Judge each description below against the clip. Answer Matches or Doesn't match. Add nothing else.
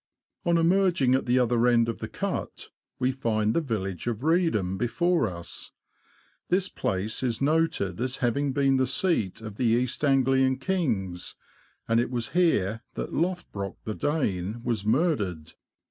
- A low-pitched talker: Matches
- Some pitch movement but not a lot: Doesn't match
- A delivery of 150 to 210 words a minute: Matches